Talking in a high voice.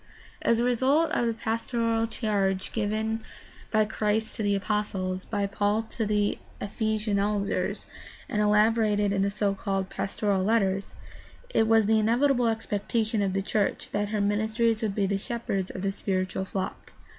Yes: high, 210 Hz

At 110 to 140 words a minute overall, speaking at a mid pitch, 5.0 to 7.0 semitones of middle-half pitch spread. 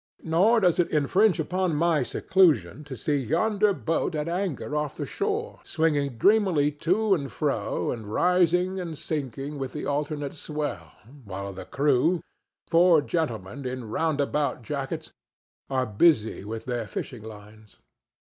Yes: slow, 135 wpm; medium, 150 Hz; wide, 5.4 semitones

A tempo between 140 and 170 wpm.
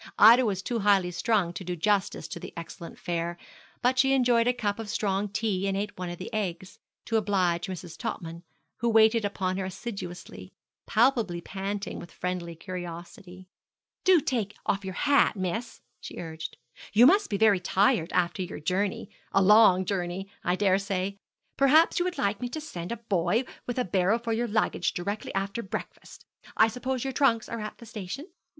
No: average, 185 wpm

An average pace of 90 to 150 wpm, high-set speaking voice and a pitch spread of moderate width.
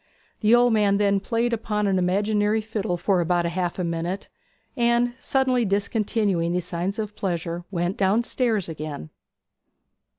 Yes: average, 140 wpm; high, 200 Hz; average, 3.8 semitones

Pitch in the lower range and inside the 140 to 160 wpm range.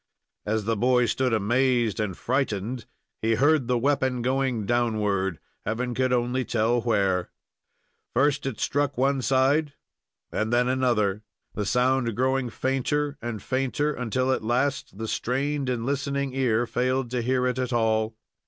Yes: low, 125 Hz; average, 150 wpm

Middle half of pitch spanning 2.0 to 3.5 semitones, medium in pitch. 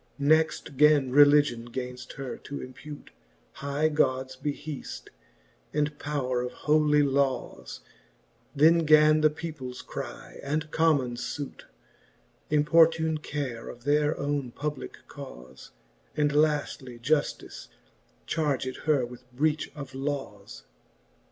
Yes: average, 2.8 semitones; medium, 145 Hz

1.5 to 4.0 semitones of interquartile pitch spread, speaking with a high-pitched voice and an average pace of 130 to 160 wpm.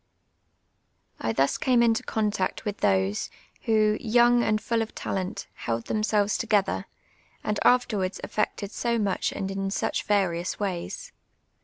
Yes: average, 3.0 semitones; high, 210 Hz; slow, 135 wpm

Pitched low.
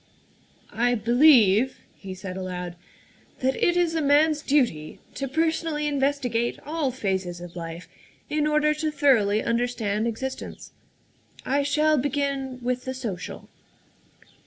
No: very high, 260 Hz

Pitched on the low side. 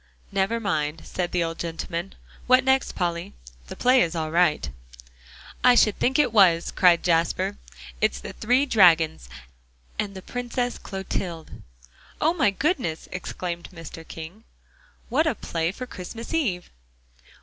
No: medium, 185 Hz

